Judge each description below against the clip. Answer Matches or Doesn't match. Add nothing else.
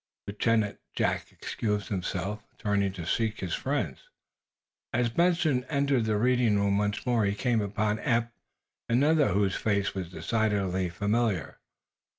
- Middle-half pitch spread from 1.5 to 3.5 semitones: Matches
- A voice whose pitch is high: Doesn't match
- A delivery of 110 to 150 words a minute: Matches